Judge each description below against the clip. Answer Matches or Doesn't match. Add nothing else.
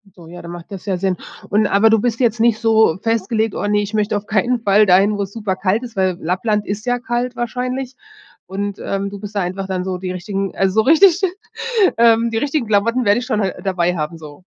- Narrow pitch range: Doesn't match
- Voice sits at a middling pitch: Doesn't match